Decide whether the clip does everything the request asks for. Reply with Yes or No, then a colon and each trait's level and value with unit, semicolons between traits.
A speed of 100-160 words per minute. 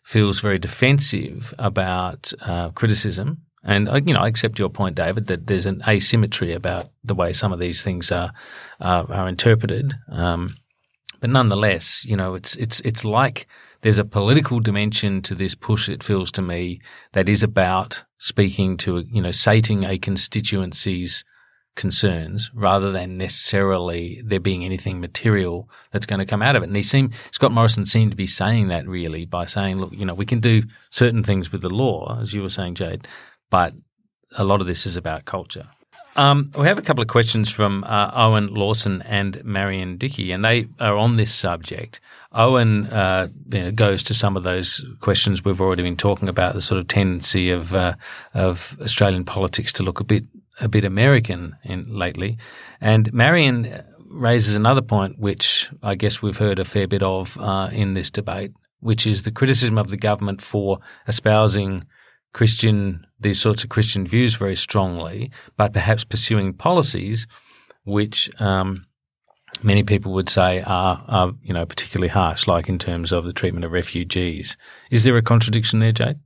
No: average, 180 wpm